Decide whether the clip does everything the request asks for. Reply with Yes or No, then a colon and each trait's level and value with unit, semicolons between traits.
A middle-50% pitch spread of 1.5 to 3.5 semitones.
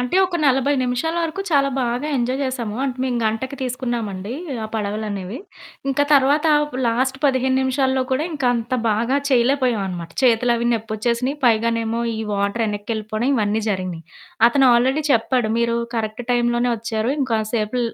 Yes: average, 3.1 semitones